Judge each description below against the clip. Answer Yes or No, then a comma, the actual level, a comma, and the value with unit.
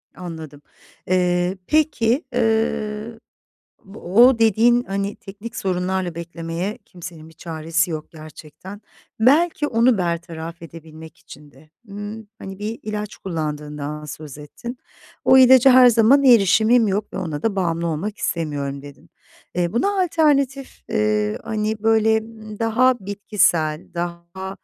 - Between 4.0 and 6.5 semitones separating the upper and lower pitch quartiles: Yes, wide, 5.4 semitones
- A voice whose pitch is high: Yes, high, 195 Hz